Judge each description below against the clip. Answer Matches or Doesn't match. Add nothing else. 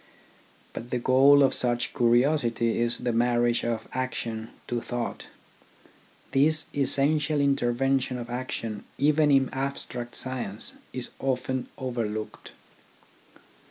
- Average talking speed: Doesn't match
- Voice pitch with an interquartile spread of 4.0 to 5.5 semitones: Doesn't match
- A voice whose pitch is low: Matches